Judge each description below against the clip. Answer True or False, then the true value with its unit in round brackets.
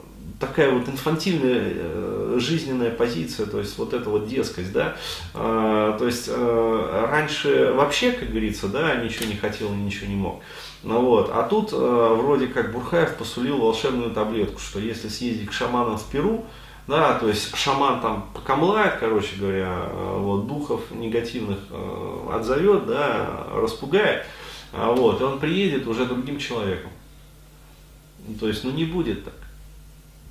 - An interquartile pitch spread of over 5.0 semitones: False (4.1 semitones)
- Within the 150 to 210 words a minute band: False (135 wpm)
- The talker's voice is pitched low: True (115 Hz)